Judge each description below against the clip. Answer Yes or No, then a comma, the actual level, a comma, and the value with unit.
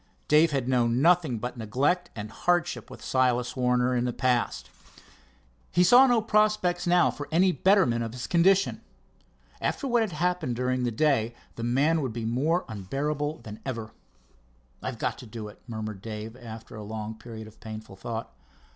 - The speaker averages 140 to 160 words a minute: No, average, 175 wpm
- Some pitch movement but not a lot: No, wide, 7.0 semitones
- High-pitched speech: No, low, 125 Hz